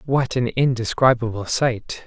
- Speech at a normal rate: No, slow, 115 wpm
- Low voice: Yes, low, 120 Hz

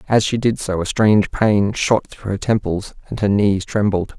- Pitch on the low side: Yes, low, 105 Hz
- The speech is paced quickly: Yes, fast, 215 wpm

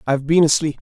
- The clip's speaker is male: Yes, male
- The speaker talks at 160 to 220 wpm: Yes, fast, 205 wpm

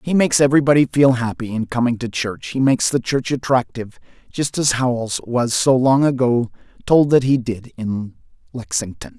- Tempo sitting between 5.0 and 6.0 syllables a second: Yes, 5.3 syllables/s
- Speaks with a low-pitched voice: Yes, low, 125 Hz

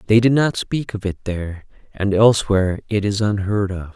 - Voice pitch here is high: No, low, 105 Hz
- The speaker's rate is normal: Yes, average, 195 wpm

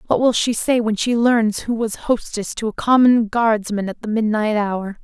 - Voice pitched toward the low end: No, high, 220 Hz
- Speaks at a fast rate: Yes, fast, 215 wpm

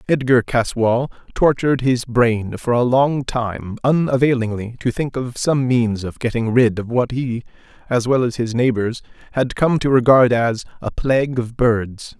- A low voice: Yes, low, 120 Hz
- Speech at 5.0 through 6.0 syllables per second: No, 4.4 syllables/s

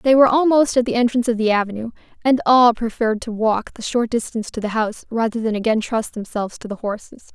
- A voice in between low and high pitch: No, high, 230 Hz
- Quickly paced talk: Yes, fast, 230 wpm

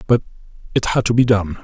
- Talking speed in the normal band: No, fast, 220 wpm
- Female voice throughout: No, male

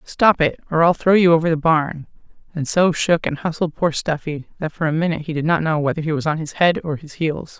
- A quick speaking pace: Yes, fast, 260 wpm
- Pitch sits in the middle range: Yes, medium, 160 Hz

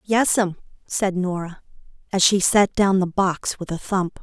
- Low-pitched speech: No, high, 190 Hz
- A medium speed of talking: Yes, average, 170 wpm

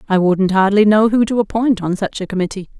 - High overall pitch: Yes, high, 200 Hz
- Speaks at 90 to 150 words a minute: No, fast, 235 wpm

